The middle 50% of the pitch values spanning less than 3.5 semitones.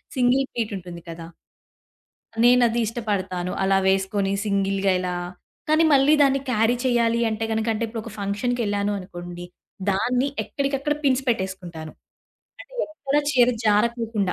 No: average, 4.4 semitones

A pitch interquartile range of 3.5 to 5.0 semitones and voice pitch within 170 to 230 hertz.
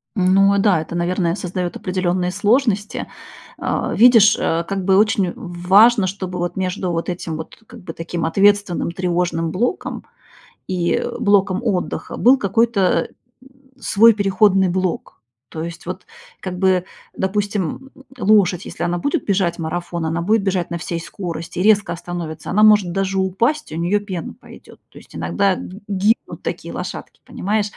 No: average, 2.9 semitones; medium, 185 Hz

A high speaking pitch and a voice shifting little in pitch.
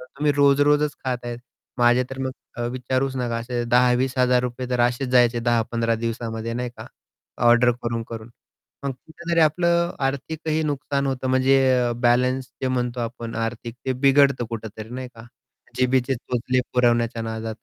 No: low, 125 Hz; narrow, 2.1 semitones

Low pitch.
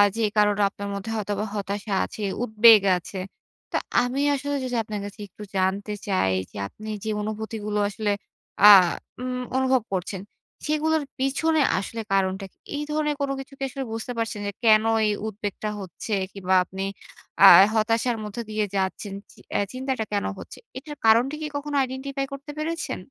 No: high, 220 Hz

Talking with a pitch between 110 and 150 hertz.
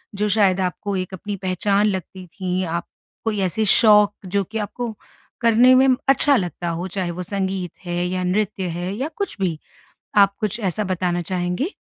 No: high, 190 Hz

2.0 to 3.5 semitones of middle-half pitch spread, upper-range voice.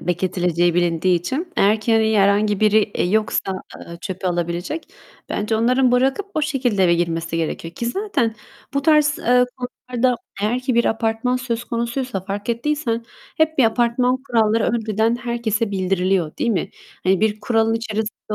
No: average, 4.4 semitones; high, 225 Hz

